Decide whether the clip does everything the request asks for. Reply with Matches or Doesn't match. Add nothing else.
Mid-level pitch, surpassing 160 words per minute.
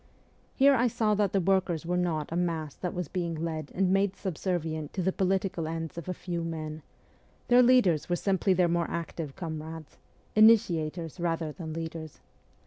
Matches